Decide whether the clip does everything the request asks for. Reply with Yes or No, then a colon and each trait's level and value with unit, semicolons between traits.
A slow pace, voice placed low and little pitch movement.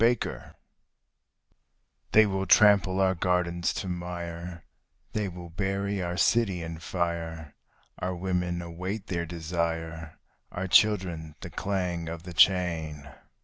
Yes: slow, 120 wpm; very low, 90 Hz; narrow, 2.1 semitones